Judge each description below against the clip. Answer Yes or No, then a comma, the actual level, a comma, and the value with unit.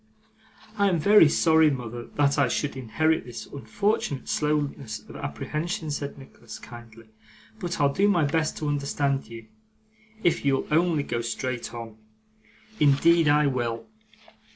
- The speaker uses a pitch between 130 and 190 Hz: Yes, medium, 140 Hz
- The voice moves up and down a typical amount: Yes, average, 4.7 semitones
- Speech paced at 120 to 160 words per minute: Yes, average, 140 wpm